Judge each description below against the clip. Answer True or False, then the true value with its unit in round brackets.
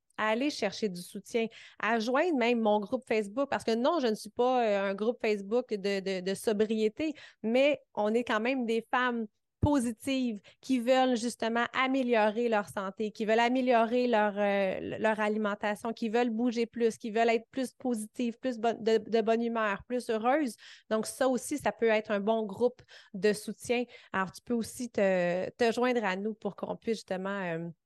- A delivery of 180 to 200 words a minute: True (190 wpm)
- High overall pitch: True (230 Hz)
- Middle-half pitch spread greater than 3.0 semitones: False (2.7 semitones)